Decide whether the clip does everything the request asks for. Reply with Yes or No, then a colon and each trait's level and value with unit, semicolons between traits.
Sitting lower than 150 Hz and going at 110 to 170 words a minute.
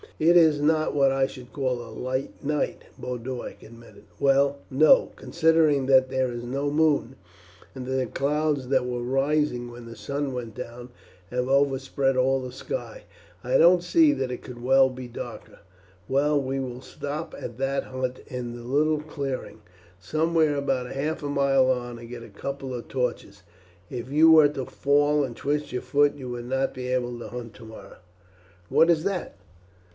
No: low, 135 Hz; average, 180 wpm